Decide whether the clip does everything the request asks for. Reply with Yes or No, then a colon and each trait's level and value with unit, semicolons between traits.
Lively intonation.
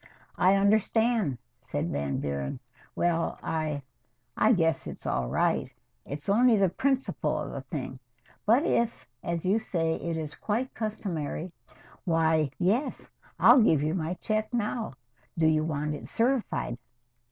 Yes: wide, 6.2 semitones